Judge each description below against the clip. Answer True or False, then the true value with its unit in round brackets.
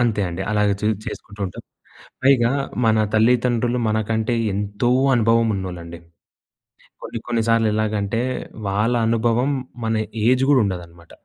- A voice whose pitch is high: False (110 Hz)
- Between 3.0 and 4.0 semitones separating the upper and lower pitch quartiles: False (2.6 semitones)